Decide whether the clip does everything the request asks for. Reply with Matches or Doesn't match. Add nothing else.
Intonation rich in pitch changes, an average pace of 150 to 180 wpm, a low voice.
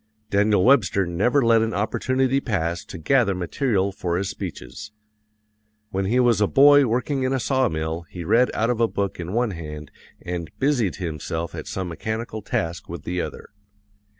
Matches